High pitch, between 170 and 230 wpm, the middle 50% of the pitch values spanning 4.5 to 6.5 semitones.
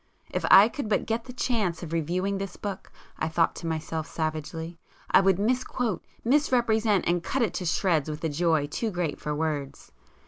No: medium, 175 Hz; average, 180 wpm; wide, 5.4 semitones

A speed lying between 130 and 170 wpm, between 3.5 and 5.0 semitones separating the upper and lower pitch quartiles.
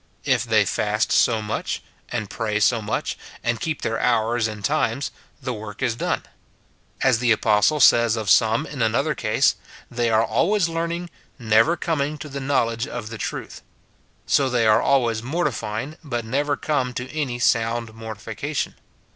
Yes: average, 165 wpm; average, 4.1 semitones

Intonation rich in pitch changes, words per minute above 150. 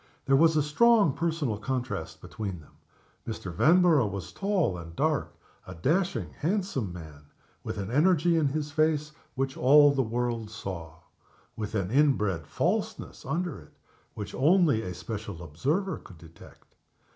No: wide, 8.4 semitones; average, 145 wpm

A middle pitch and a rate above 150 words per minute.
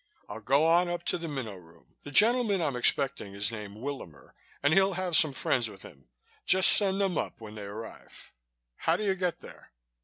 Yes: medium, 145 Hz; fast, 205 wpm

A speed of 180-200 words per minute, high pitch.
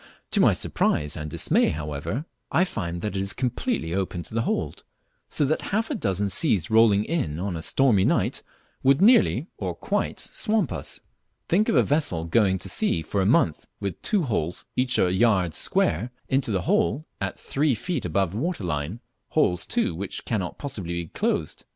No: average, 190 wpm; low, 100 Hz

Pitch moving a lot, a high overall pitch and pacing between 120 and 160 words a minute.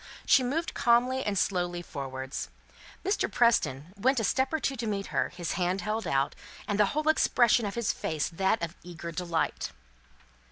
No: wide, 5.8 semitones; high, 200 Hz; average, 175 wpm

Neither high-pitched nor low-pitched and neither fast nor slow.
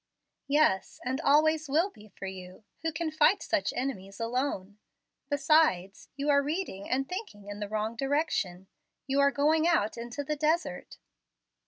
No: very high, 275 Hz; average, 160 wpm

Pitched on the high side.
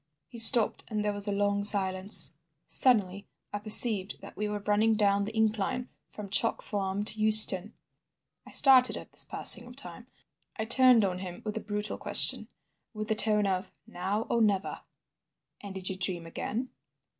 Yes: high, 210 Hz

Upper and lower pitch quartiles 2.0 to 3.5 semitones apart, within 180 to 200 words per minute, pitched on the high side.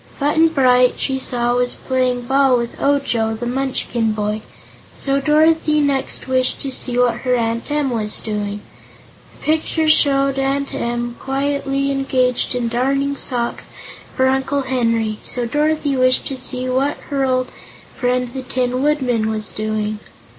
No: narrow, 2.5 semitones; average, 150 wpm; very high, 255 Hz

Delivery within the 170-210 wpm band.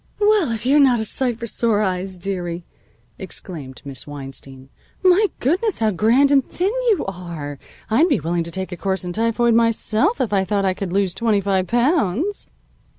Yes: average, 185 wpm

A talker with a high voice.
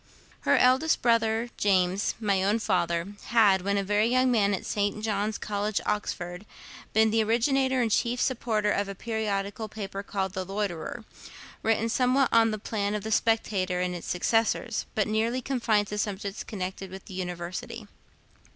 Yes: high, 210 Hz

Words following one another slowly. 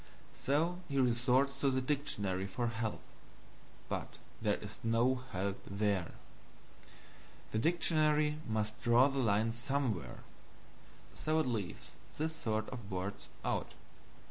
Yes: slow, 120 wpm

